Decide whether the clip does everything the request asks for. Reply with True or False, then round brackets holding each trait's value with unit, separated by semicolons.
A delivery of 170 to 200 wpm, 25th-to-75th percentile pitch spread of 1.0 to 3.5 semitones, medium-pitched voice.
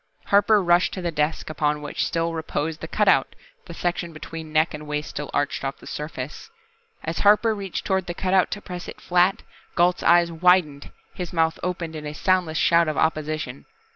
True (190 wpm; 2.7 semitones; 165 Hz)